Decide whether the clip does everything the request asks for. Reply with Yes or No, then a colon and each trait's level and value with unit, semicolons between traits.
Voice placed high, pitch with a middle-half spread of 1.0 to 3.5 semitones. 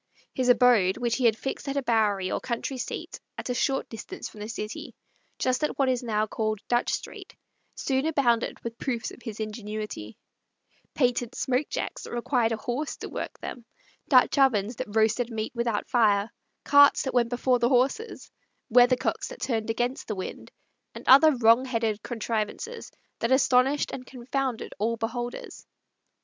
Yes: high, 240 Hz; average, 2.7 semitones